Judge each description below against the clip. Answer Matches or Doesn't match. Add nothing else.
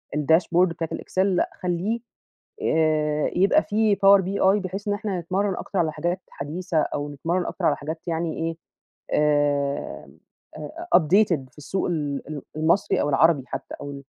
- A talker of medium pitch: Matches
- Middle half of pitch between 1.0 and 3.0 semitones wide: Doesn't match